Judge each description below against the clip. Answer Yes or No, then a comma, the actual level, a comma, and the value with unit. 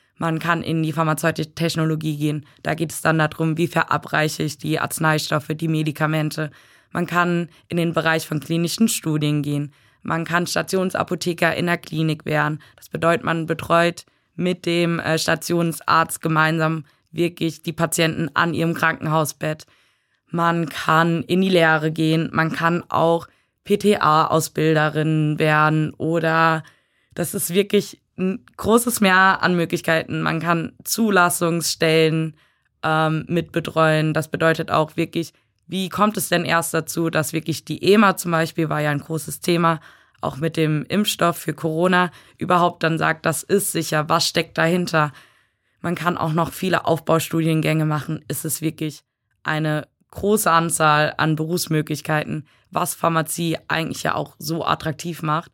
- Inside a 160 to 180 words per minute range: No, average, 145 wpm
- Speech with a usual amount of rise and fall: No, narrow, 1.6 semitones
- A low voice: No, medium, 160 Hz